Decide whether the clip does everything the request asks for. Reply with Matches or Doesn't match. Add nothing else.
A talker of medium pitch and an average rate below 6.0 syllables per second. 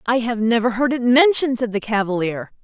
Doesn't match